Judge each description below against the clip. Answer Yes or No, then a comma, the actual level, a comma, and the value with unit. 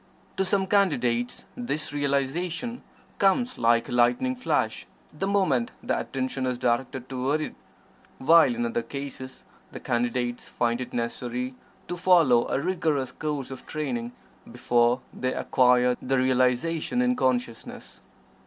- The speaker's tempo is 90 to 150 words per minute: Yes, slow, 135 wpm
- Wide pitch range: Yes, wide, 5.8 semitones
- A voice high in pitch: No, low, 130 Hz